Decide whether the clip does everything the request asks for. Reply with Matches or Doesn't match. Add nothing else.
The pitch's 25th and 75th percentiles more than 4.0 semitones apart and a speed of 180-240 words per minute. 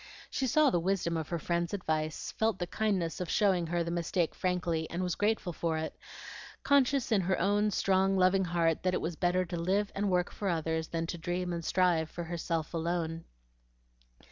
Doesn't match